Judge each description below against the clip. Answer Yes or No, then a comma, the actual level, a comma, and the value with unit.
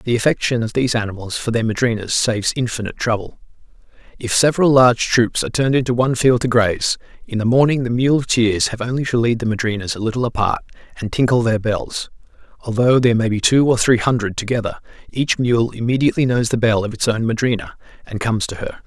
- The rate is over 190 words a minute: Yes, average, 200 wpm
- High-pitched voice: No, low, 115 Hz